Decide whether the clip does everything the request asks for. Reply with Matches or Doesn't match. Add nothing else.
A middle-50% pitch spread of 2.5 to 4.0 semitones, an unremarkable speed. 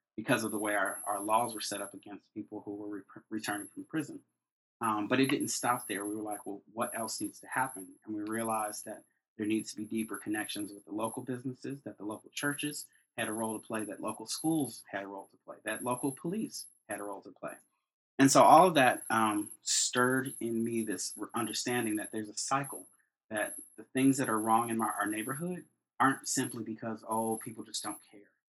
Doesn't match